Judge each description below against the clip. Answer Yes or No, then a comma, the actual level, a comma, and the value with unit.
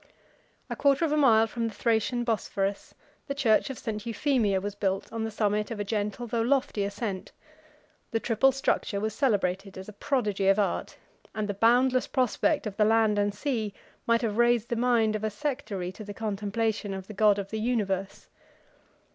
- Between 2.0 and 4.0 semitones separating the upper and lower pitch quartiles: Yes, average, 2.8 semitones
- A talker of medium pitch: No, high, 220 Hz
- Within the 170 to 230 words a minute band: Yes, average, 190 wpm